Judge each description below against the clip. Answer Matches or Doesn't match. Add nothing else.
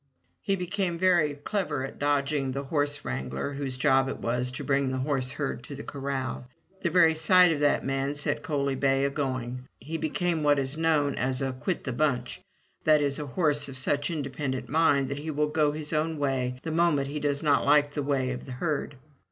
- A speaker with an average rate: Doesn't match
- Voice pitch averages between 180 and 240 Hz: Doesn't match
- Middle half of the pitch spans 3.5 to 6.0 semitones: Doesn't match